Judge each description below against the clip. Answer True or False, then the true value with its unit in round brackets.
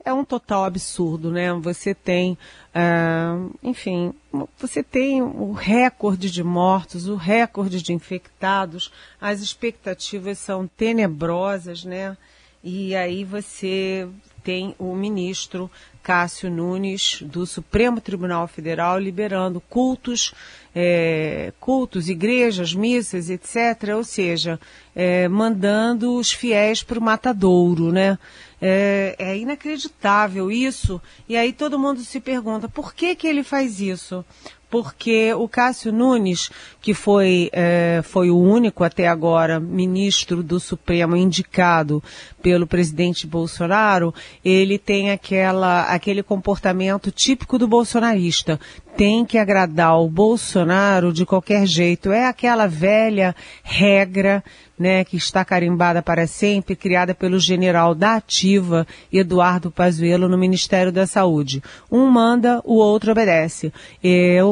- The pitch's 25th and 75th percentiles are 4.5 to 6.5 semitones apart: False (3.5 semitones)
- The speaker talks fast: False (120 wpm)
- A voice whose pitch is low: False (190 Hz)